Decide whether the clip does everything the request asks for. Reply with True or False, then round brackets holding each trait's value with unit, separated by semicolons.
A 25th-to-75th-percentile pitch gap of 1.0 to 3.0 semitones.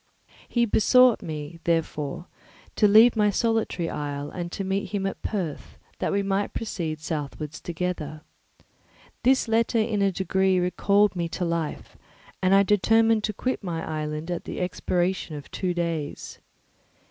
False (4.2 semitones)